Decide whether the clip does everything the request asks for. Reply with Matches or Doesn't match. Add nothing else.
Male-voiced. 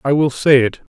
Matches